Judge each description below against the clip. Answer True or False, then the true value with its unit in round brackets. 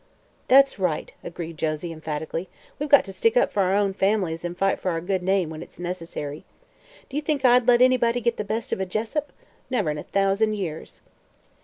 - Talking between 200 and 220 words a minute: True (205 wpm)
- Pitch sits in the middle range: False (195 Hz)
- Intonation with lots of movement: True (5.8 semitones)